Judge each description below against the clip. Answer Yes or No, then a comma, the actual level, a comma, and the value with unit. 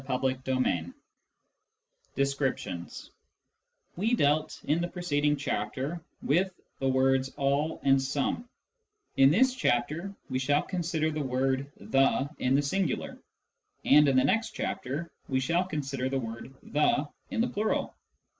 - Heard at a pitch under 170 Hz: Yes, medium, 140 Hz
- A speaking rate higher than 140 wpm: No, slow, 135 wpm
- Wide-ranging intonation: No, average, 4.0 semitones